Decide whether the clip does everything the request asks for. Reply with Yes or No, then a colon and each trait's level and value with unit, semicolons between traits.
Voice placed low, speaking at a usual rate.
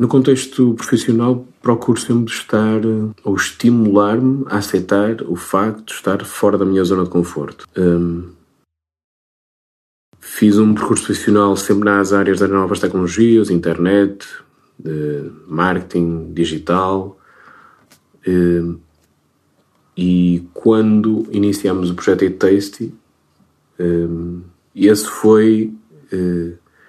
No: low, 100 Hz; slow, 105 wpm